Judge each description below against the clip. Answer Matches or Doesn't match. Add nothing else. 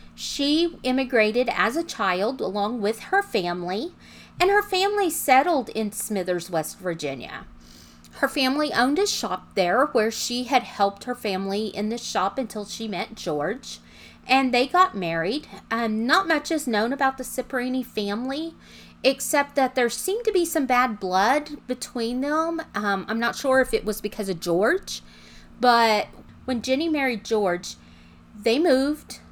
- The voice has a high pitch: Matches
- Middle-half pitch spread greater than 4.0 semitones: Matches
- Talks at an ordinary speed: Matches